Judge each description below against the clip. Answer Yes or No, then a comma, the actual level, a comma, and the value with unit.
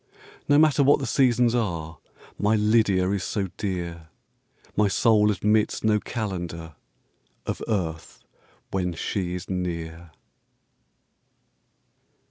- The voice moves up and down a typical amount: Yes, average, 4.1 semitones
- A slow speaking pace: Yes, slow, 105 wpm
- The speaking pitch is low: Yes, low, 100 Hz